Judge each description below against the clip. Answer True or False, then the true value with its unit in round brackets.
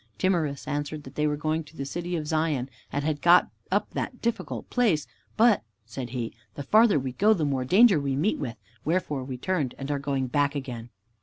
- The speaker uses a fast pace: True (210 wpm)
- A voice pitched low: False (145 Hz)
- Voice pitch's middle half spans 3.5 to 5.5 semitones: True (4.3 semitones)